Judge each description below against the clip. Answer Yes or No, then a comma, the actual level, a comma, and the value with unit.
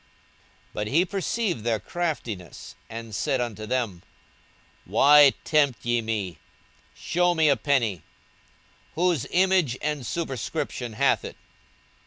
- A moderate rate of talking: No, slow, 125 wpm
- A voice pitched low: Yes, low, 130 Hz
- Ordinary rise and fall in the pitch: No, wide, 6.4 semitones